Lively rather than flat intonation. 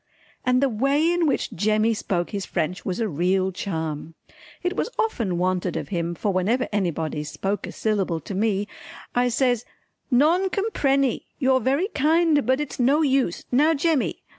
Yes: wide, 7.1 semitones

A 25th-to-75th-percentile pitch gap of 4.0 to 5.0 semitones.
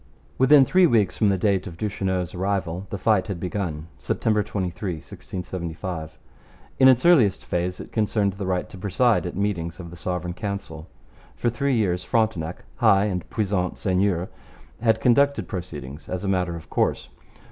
No: average, 3.3 semitones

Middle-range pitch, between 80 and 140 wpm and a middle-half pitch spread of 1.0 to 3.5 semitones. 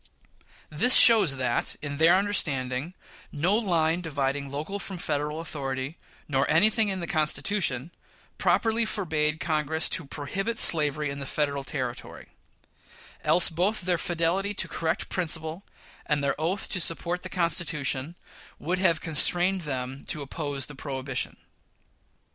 No: medium, 160 Hz; slow, 135 wpm; average, 4.1 semitones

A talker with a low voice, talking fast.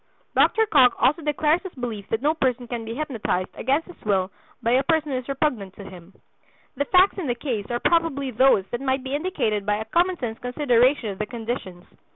No: very high, 255 Hz; fast, 210 wpm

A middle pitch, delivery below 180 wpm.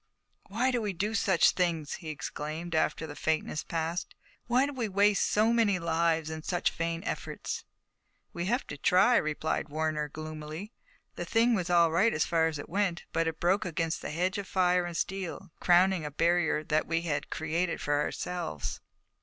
No: medium, 170 Hz; average, 185 wpm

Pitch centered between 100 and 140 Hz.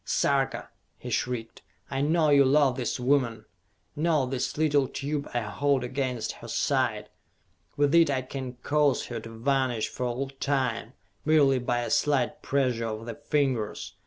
Yes: low, 135 Hz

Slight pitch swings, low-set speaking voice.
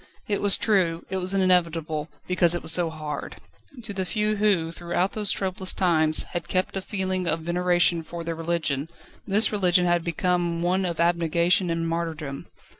No: narrow, 2.1 semitones; medium, 175 Hz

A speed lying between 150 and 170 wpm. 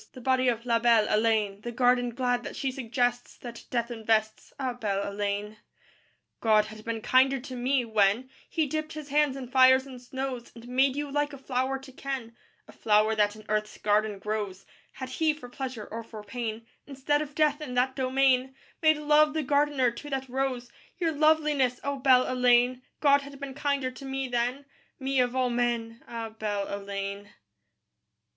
No: average, 185 wpm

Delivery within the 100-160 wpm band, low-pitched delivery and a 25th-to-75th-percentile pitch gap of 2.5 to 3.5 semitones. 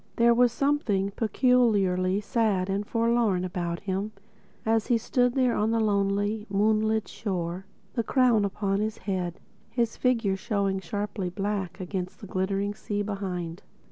No: average, 140 wpm; high, 205 Hz; average, 2.9 semitones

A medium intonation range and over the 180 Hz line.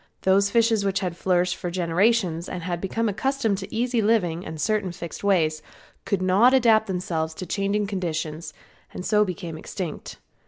Yes: average, 3.5 semitones; high, 190 Hz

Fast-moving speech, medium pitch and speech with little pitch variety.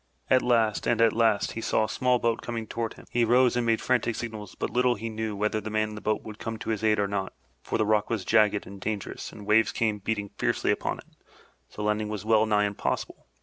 No: fast, 255 wpm; low, 110 Hz; narrow, 1.6 semitones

